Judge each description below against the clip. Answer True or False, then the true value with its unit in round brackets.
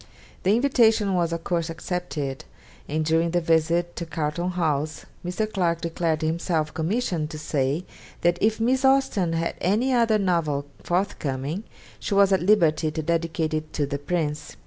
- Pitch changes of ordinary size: True (3.5 semitones)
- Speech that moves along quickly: False (160 wpm)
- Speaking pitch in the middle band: True (170 Hz)